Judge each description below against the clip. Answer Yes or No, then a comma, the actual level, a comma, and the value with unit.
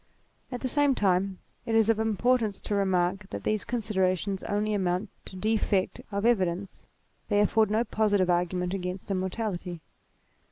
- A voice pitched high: Yes, high, 200 Hz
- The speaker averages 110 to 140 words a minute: No, average, 150 wpm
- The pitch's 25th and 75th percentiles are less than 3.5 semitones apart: Yes, average, 2.9 semitones